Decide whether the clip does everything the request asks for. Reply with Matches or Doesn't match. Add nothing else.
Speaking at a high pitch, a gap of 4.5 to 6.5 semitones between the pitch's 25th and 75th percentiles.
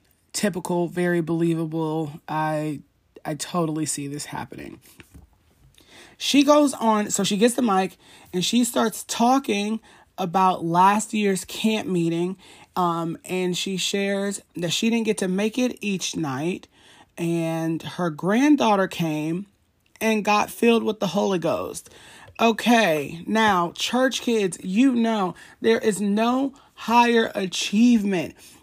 Matches